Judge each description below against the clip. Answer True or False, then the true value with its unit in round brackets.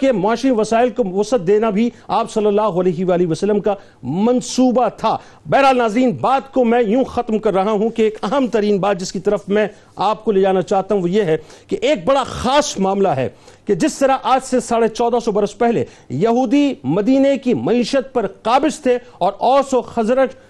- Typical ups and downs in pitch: True (3.8 semitones)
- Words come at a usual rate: False (210 wpm)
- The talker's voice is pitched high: True (230 Hz)